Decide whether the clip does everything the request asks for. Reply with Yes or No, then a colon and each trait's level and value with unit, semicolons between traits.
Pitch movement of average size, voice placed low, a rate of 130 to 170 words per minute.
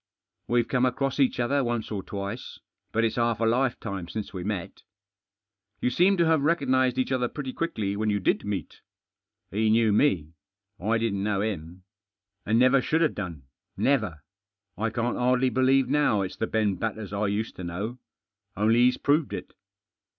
No: average, 4.1 semitones; low, 115 Hz; average, 180 wpm